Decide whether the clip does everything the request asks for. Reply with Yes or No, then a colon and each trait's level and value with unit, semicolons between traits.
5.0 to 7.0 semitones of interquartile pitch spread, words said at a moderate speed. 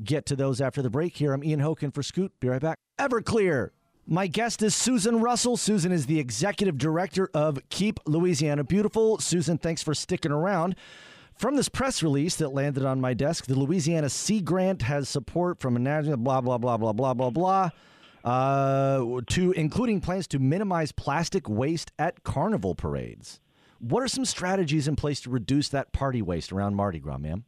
Yes: wide, 5.4 semitones; average, 185 wpm